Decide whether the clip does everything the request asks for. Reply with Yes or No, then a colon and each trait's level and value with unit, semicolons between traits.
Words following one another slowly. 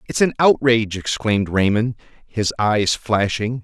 Yes: slow, 130 wpm